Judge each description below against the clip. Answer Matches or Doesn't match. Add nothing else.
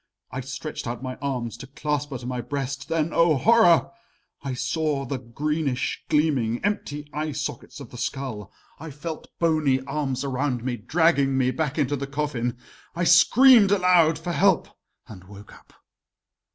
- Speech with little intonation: Doesn't match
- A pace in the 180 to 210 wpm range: Doesn't match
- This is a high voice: Doesn't match